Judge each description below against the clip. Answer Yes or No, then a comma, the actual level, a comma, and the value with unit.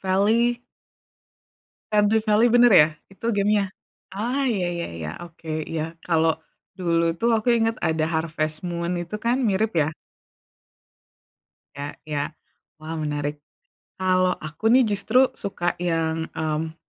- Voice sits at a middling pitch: Yes, medium, 175 Hz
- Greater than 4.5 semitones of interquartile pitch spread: Yes, average, 5.2 semitones